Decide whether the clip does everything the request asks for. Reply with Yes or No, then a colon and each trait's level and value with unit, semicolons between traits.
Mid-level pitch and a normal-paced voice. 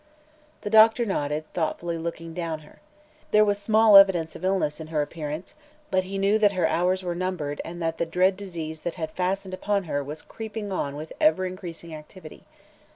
Yes: medium, 180 Hz; average, 190 wpm